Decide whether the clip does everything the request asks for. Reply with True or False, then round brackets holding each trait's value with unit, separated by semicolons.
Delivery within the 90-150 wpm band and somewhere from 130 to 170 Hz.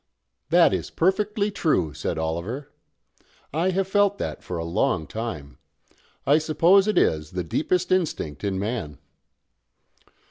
True (135 wpm; 140 Hz)